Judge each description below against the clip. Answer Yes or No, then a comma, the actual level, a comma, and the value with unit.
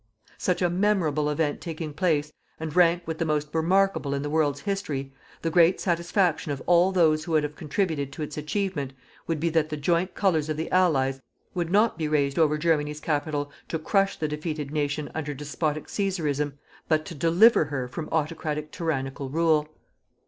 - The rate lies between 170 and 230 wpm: Yes, average, 180 wpm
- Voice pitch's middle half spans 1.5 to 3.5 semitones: Yes, narrow, 2.6 semitones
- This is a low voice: No, medium, 155 Hz